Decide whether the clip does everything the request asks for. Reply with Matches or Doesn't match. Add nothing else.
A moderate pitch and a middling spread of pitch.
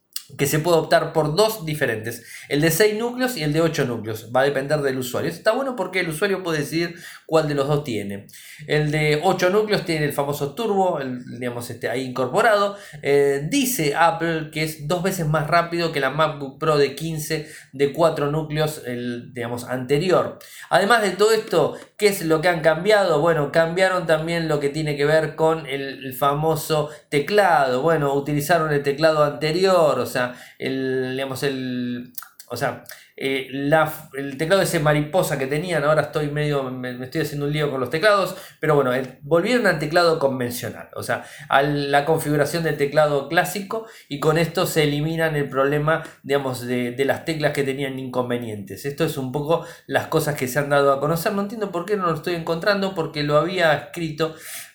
Matches